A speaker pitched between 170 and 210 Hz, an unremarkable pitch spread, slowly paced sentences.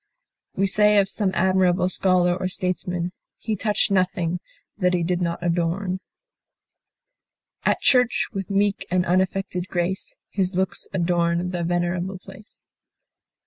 No: medium, 185 Hz; narrow, 1.7 semitones; slow, 130 wpm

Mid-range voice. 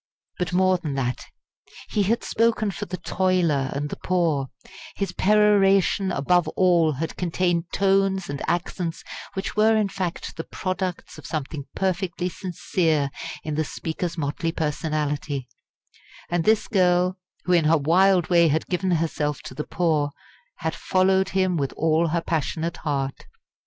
Yes: medium, 175 Hz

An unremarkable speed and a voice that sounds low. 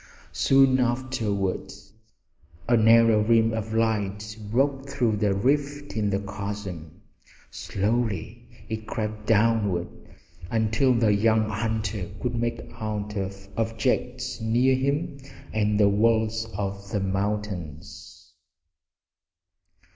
No: slow, 100 wpm; low, 110 Hz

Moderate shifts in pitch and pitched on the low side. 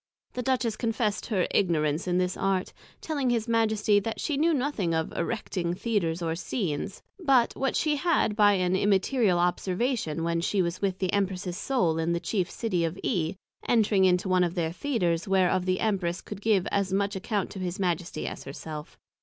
No: average, 4.2 semitones; high, 190 Hz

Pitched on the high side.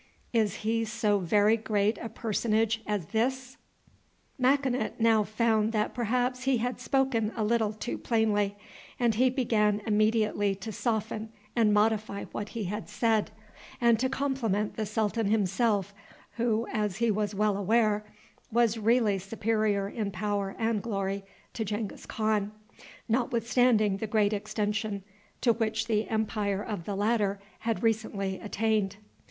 Yes: high, 220 Hz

